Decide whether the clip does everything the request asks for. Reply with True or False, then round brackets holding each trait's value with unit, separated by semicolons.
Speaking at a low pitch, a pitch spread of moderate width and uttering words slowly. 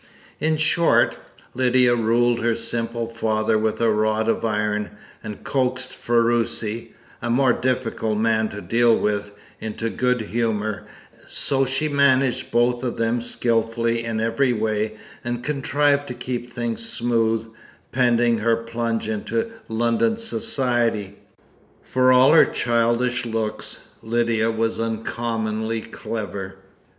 False (115 Hz; 1.9 semitones; 125 wpm)